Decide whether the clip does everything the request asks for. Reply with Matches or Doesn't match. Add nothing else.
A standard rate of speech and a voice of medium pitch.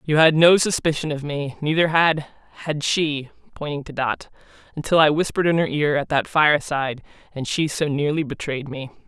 Matches